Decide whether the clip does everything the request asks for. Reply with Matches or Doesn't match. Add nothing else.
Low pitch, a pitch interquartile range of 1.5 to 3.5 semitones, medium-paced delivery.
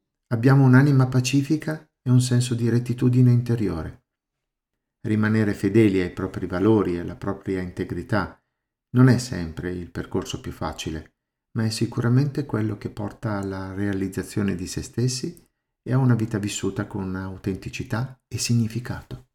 Doesn't match